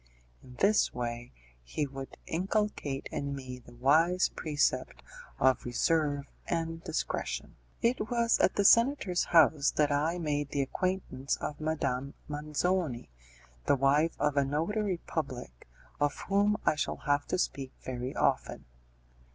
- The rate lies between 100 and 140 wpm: Yes, slow, 135 wpm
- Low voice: No, medium, 150 Hz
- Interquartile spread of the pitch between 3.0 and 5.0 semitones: Yes, average, 4.6 semitones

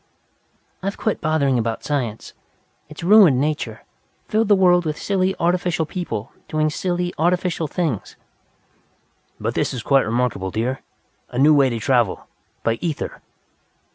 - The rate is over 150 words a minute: No, average, 140 wpm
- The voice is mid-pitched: Yes, medium, 155 Hz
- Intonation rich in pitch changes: Yes, wide, 6.0 semitones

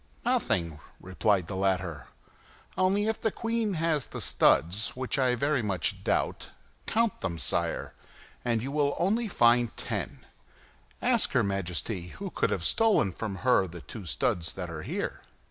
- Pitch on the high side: No, low, 115 Hz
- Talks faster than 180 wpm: No, average, 155 wpm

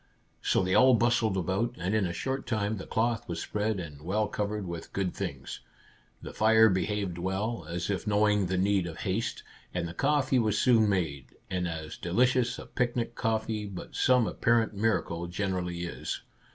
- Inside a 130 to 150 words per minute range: No, average, 180 wpm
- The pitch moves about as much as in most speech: Yes, average, 4.0 semitones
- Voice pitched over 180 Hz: No, low, 105 Hz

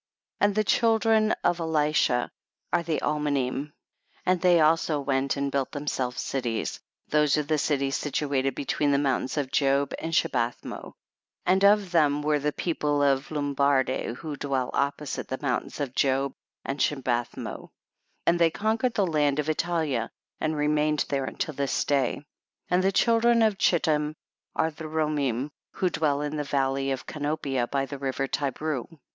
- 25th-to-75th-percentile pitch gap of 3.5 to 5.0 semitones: No, average, 2.7 semitones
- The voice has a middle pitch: Yes, medium, 145 Hz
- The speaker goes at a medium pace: Yes, average, 165 wpm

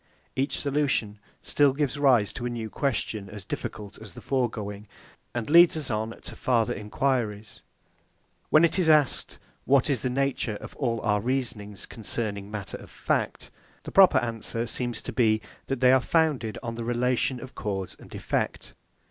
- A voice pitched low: Yes, low, 120 Hz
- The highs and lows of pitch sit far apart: No, average, 4.1 semitones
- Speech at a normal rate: Yes, average, 170 wpm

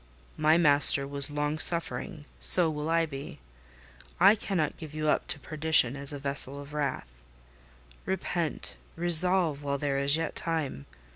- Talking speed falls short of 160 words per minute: Yes, average, 145 wpm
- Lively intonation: No, narrow, 2.5 semitones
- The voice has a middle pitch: Yes, medium, 150 Hz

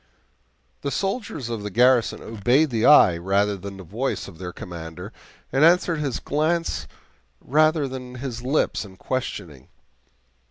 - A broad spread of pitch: Yes, wide, 6.8 semitones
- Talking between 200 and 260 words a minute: No, average, 145 wpm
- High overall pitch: No, low, 125 Hz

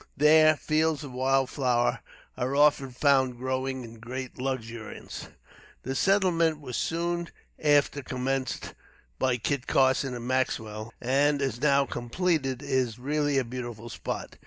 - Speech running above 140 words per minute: No, slow, 135 wpm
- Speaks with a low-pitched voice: Yes, low, 130 Hz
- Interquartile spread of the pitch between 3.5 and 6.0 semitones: No, average, 2.7 semitones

